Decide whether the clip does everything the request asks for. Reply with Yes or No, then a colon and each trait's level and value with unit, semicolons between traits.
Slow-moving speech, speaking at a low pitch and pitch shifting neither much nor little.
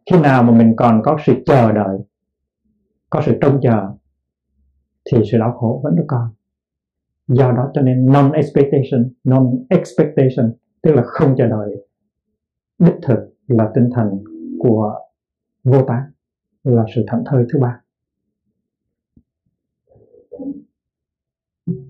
Yes: slow, 120 wpm; low, 125 Hz; average, 4.5 semitones